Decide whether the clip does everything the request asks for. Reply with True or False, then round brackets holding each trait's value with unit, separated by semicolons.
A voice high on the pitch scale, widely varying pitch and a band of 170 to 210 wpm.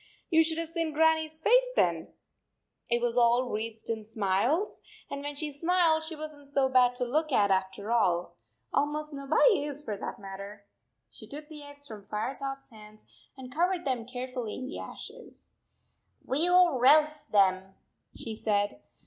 True (270 Hz; 5.9 semitones; 180 wpm)